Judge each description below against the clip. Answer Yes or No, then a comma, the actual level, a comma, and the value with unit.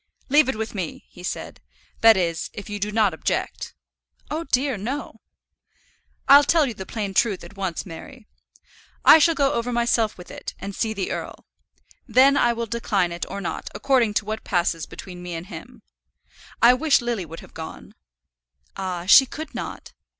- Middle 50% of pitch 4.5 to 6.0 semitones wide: Yes, average, 5.3 semitones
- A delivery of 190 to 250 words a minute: No, average, 180 wpm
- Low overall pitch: No, high, 215 Hz